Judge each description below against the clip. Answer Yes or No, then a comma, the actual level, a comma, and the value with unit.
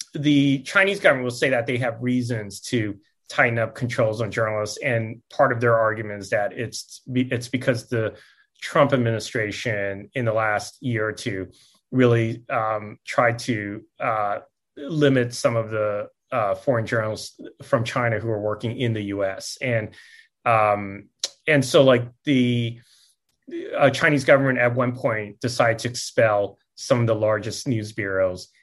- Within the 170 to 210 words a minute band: No, average, 155 wpm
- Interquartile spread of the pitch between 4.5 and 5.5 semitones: No, average, 3.1 semitones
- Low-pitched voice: Yes, low, 120 Hz